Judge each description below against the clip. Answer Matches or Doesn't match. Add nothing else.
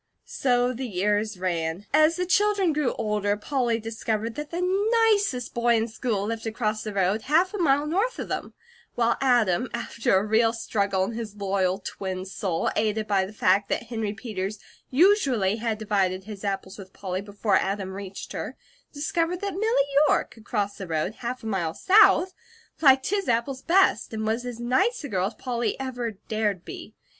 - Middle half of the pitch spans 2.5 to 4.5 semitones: Doesn't match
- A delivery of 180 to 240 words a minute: Matches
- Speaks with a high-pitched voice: Matches